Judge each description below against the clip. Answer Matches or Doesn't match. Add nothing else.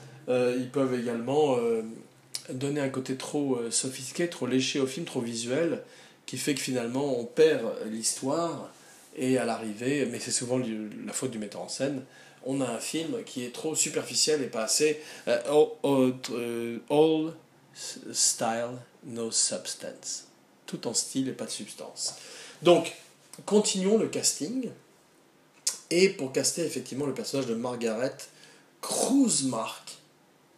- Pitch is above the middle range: Doesn't match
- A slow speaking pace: Matches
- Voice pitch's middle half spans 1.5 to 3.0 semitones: Doesn't match